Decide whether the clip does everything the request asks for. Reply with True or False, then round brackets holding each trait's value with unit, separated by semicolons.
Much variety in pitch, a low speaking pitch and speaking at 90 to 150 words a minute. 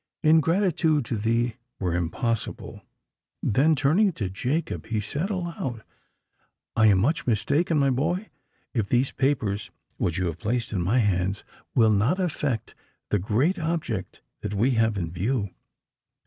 True (6.9 semitones; 120 Hz; 140 wpm)